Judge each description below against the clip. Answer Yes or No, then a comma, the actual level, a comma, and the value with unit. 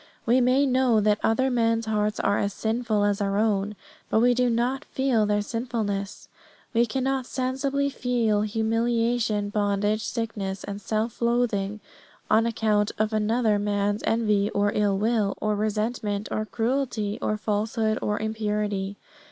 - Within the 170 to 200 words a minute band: No, average, 145 wpm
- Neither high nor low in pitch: No, high, 215 Hz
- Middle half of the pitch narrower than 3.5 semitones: Yes, narrow, 2.4 semitones